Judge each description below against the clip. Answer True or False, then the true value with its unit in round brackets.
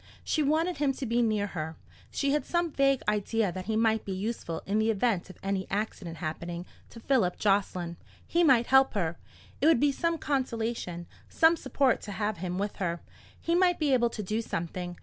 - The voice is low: False (220 Hz)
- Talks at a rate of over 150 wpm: True (200 wpm)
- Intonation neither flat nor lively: False (6.5 semitones)